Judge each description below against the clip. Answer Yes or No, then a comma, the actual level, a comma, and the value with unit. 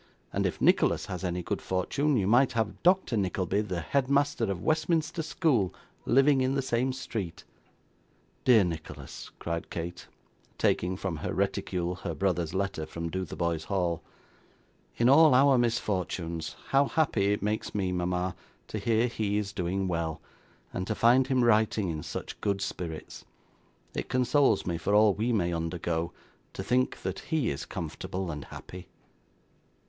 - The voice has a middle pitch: No, low, 100 Hz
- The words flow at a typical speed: Yes, average, 155 wpm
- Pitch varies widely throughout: Yes, wide, 6.1 semitones